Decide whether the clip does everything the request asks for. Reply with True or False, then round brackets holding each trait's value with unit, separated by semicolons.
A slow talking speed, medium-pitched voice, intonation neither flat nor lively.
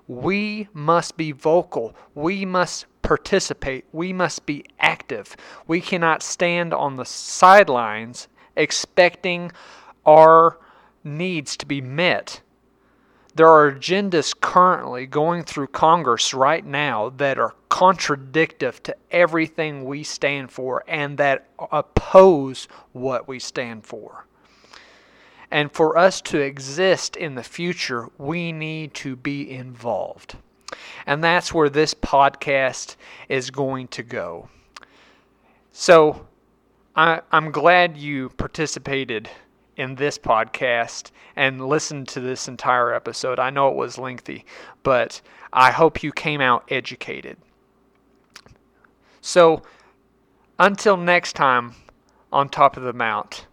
True (120 wpm; 150 Hz; 4.2 semitones)